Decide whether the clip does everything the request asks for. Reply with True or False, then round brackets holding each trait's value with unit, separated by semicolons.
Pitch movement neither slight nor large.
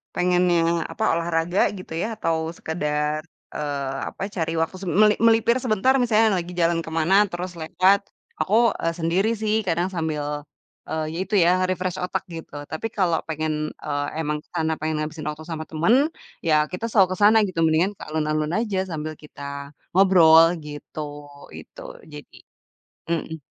True (3.0 semitones)